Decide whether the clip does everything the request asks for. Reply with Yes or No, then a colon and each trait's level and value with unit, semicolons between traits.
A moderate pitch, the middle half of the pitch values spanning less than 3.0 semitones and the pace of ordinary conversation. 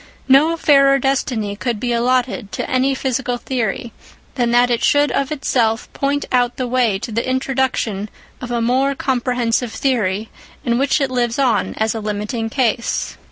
No: high, 245 Hz; narrow, 2.6 semitones; average, 165 wpm